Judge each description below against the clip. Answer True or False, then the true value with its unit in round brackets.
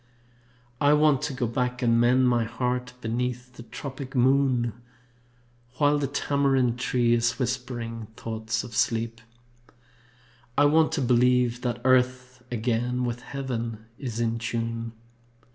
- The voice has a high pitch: False (125 Hz)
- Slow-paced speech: True (130 wpm)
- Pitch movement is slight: True (1.8 semitones)